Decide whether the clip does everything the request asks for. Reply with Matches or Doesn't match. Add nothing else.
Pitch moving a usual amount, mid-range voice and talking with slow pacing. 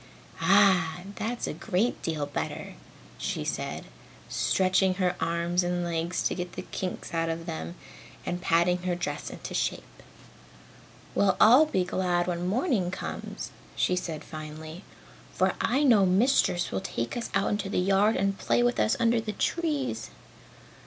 Doesn't match